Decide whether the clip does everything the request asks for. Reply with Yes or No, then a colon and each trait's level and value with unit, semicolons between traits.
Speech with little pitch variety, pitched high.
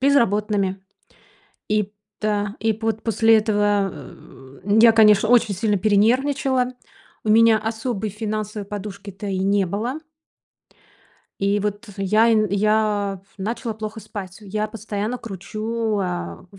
Yes: narrow, 1.8 semitones; high, 210 Hz